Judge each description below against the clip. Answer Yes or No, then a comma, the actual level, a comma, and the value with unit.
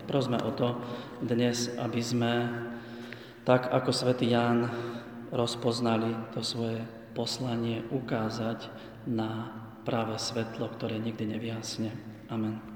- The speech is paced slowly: Yes, slow, 105 wpm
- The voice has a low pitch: Yes, low, 115 Hz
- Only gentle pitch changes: Yes, narrow, 1.1 semitones